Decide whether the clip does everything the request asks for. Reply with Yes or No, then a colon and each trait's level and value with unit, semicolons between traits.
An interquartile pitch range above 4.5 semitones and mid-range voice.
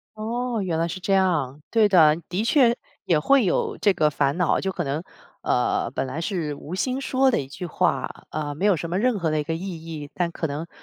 Yes: average, 5.1 semitones; medium, 170 Hz